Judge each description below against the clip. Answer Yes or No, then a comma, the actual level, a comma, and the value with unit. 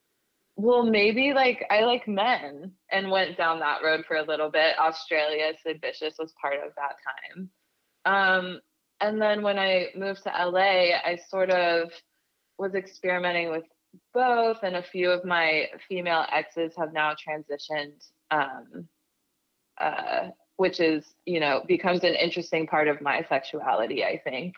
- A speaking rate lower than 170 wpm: Yes, average, 155 wpm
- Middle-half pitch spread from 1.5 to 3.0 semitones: No, average, 3.4 semitones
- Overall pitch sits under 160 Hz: No, medium, 175 Hz